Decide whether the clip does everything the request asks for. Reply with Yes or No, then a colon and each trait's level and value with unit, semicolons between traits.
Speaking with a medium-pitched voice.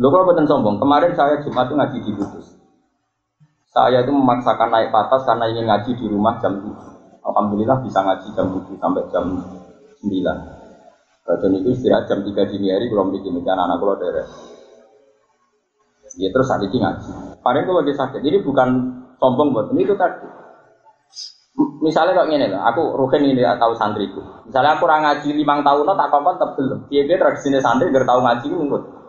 No: low, 130 Hz